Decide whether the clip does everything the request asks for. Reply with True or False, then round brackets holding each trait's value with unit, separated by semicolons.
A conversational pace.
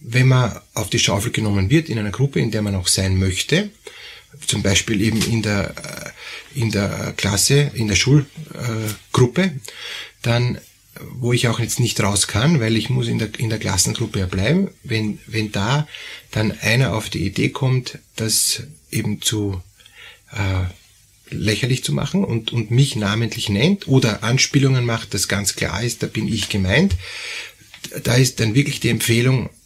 True (170 wpm)